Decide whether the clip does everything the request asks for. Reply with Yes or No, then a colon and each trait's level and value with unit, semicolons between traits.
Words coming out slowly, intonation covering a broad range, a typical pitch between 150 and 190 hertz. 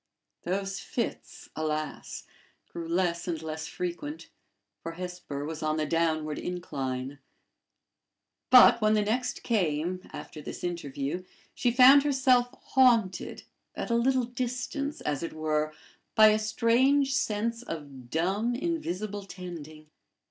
Yes: slow, 125 wpm; wide, 7.2 semitones; medium, 185 Hz